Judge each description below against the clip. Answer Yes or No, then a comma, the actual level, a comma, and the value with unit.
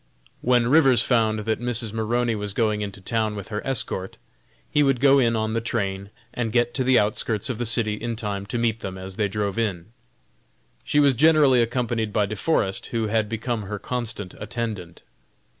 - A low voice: Yes, low, 110 Hz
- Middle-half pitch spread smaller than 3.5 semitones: Yes, average, 2.7 semitones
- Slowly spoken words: No, average, 190 wpm